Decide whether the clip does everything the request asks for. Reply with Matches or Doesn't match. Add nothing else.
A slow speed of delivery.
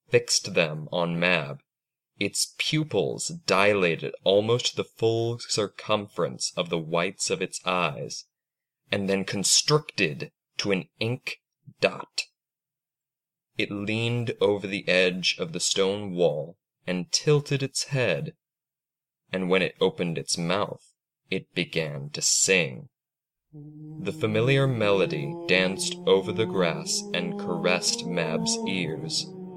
Matches